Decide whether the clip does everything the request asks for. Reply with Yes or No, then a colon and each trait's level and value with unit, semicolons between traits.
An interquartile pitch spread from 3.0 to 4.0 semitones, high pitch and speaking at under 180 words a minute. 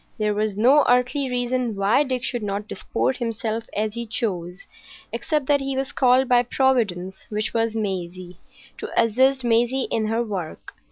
Yes: average, 3.6 semitones; high, 230 Hz; average, 165 wpm